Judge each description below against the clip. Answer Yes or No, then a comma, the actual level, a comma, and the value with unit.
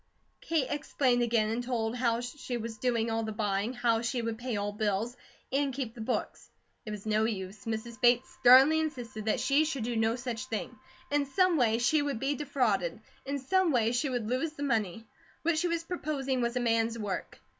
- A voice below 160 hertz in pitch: No, high, 240 Hz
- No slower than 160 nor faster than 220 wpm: Yes, fast, 205 wpm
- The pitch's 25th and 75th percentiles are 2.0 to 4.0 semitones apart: Yes, average, 3.6 semitones